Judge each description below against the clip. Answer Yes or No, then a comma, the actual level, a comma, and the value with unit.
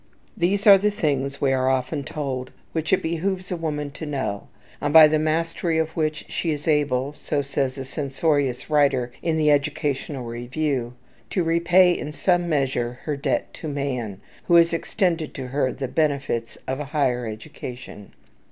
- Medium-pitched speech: Yes, medium, 145 Hz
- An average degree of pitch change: Yes, average, 3.6 semitones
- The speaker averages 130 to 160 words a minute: No, average, 170 wpm